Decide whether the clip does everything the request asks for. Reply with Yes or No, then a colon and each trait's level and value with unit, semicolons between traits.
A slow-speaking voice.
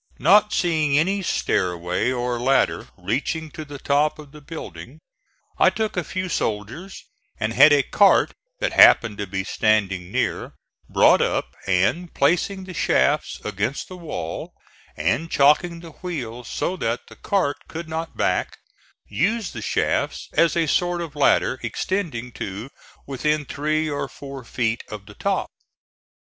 No: average, 150 wpm